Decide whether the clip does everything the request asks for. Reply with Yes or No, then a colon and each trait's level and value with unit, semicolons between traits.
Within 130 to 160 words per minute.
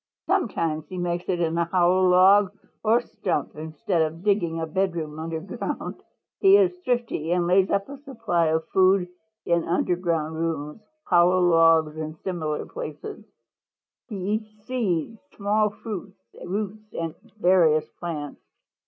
Yes: average, 140 wpm